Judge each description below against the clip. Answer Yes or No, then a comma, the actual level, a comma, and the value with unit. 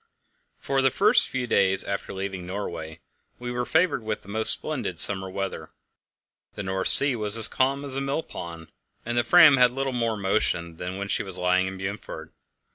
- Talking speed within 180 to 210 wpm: Yes, average, 185 wpm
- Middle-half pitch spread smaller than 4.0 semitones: No, average, 5.2 semitones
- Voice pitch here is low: Yes, low, 105 Hz